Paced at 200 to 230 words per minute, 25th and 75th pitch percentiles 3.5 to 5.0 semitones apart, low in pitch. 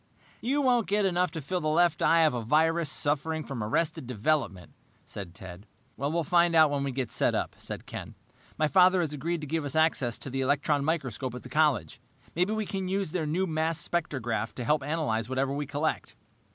No: fast, 205 wpm; average, 4.2 semitones; medium, 155 Hz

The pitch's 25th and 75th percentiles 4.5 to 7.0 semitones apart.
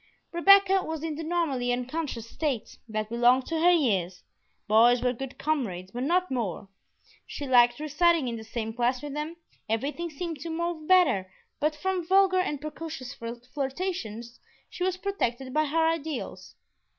Yes: wide, 5.5 semitones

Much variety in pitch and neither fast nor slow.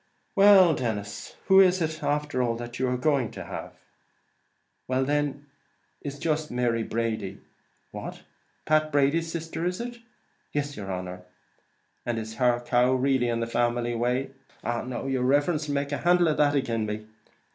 No: average, 4.2 semitones; average, 170 wpm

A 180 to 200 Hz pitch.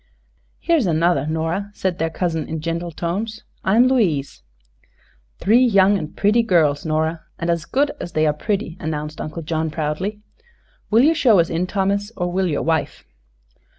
No: medium, 170 Hz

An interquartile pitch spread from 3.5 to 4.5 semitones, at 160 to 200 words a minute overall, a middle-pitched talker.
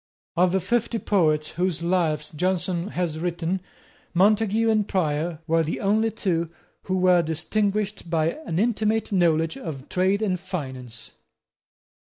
No: average, 3.8 semitones; slow, 135 wpm; medium, 180 Hz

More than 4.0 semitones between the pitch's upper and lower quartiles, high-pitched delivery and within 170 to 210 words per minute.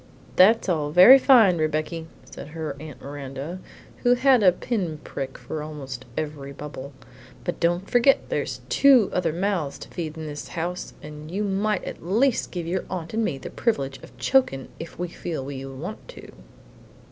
No: average, 5.3 semitones; medium, 165 Hz; average, 175 wpm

